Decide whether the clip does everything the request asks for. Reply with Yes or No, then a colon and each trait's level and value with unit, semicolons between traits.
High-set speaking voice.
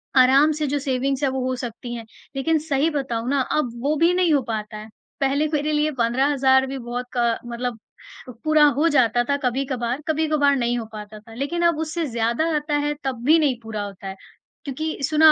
Yes: very high, 270 Hz